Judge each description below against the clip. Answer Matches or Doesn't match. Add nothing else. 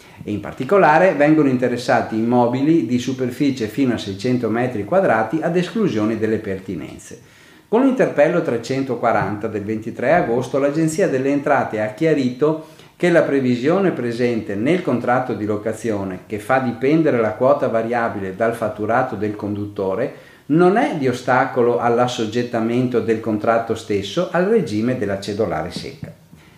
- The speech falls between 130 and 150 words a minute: Matches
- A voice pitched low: Matches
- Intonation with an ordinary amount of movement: Matches